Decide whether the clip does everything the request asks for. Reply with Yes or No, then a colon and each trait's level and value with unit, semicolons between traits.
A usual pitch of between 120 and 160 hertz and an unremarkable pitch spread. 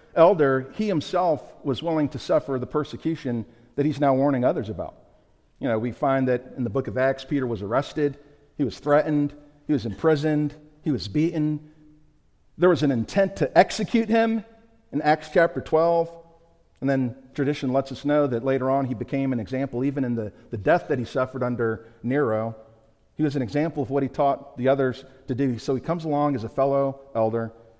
Yes: medium, 140 Hz; average, 3.1 semitones